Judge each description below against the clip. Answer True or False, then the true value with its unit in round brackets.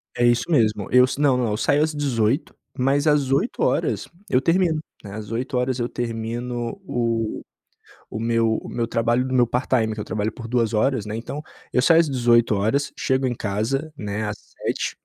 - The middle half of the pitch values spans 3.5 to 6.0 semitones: False (3.1 semitones)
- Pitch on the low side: True (120 Hz)